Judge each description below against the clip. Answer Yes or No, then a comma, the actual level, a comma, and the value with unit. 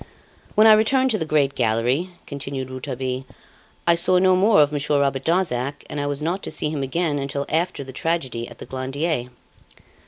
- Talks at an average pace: Yes, average, 190 wpm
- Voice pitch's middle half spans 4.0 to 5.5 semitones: Yes, average, 4.4 semitones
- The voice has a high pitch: No, medium, 145 Hz